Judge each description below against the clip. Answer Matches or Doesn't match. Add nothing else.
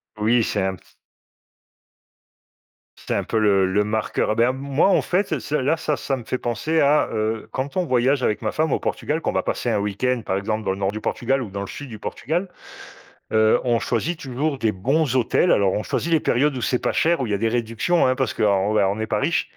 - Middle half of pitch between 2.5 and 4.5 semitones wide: Doesn't match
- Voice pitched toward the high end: Doesn't match